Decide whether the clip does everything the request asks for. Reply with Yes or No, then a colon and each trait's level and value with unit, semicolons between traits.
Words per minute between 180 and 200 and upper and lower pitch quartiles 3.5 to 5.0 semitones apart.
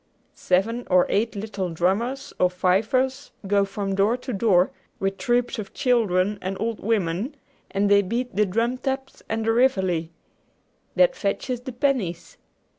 No: average, 150 wpm; average, 4.3 semitones